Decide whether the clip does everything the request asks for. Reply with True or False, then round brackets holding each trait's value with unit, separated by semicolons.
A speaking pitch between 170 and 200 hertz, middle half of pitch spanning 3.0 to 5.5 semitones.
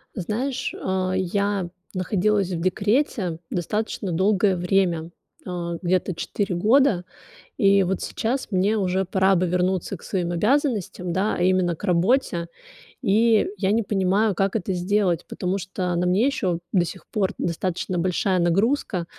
False (190 Hz; 2.6 semitones)